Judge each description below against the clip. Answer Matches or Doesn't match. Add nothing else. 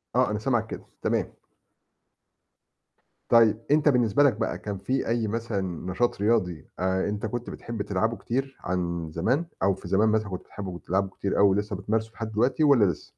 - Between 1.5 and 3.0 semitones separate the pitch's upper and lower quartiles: Doesn't match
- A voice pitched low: Matches